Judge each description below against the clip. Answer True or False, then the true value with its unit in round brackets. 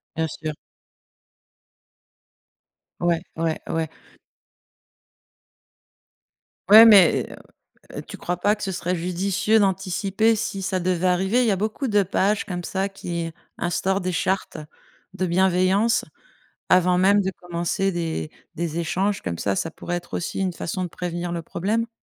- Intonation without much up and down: True (2.3 semitones)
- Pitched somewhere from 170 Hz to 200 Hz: True (185 Hz)